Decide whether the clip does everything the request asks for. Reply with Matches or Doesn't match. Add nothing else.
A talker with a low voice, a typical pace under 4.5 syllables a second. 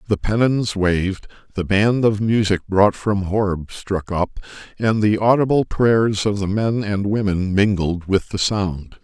Matches